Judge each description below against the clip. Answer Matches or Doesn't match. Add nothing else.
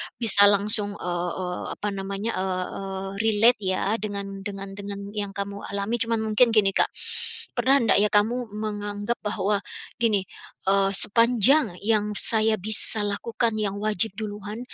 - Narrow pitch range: Matches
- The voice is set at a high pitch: Matches